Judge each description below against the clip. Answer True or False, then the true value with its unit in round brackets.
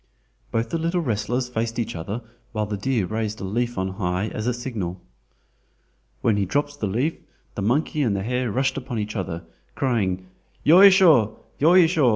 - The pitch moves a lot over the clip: False (4.7 semitones)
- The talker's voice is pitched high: False (115 Hz)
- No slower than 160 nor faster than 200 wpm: True (170 wpm)